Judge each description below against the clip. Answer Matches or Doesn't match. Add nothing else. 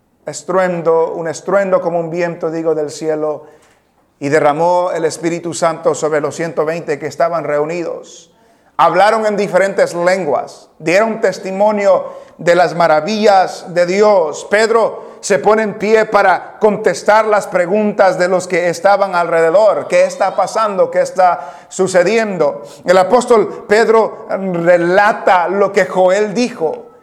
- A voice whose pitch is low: Doesn't match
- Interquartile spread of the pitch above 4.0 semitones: Doesn't match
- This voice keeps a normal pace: Doesn't match